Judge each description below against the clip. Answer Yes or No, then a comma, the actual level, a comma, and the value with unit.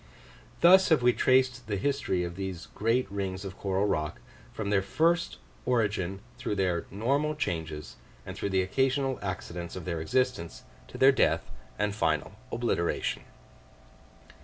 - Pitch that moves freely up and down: Yes, wide, 6.1 semitones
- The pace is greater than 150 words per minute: No, average, 145 wpm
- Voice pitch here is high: No, low, 100 Hz